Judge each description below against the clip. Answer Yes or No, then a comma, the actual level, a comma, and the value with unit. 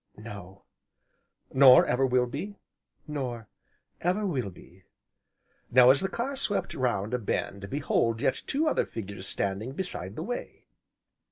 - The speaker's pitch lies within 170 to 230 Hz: No, low, 125 Hz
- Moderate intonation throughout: No, wide, 7.3 semitones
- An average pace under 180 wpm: Yes, average, 140 wpm